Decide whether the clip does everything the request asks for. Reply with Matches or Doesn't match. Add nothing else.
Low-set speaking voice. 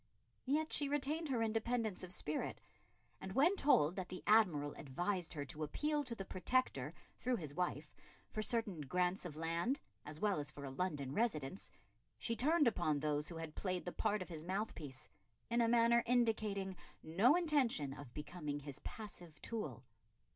Doesn't match